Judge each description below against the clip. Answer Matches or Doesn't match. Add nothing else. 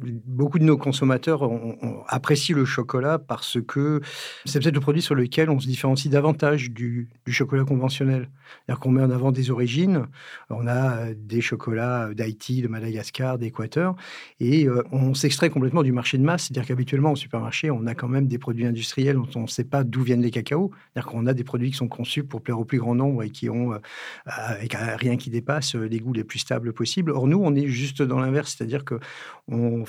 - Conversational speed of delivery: Matches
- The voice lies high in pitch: Doesn't match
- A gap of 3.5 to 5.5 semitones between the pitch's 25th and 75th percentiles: Doesn't match